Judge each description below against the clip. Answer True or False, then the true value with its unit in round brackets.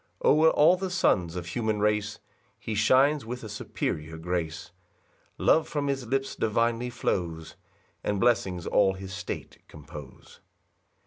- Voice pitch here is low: True (105 Hz)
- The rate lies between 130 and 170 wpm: True (140 wpm)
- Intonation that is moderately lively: False (6.4 semitones)